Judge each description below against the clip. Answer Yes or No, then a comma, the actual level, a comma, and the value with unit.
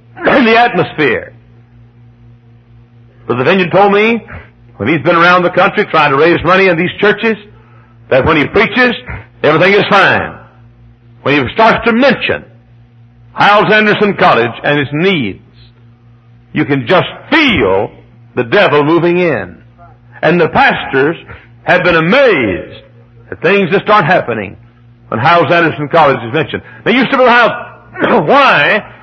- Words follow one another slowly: No, average, 145 wpm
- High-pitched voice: No, medium, 140 Hz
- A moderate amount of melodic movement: No, wide, 7.8 semitones